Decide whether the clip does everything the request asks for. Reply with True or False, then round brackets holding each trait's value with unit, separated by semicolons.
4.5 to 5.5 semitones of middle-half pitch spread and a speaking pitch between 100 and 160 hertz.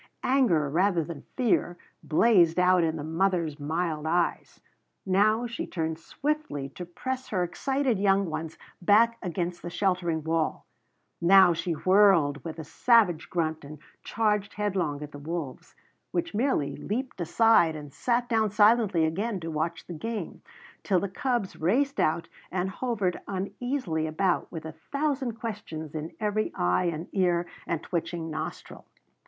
False (5.1 semitones; 180 Hz)